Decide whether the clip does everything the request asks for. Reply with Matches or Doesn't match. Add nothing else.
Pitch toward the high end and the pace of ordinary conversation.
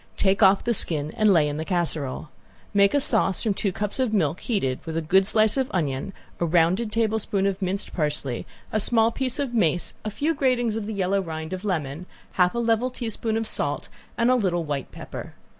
Doesn't match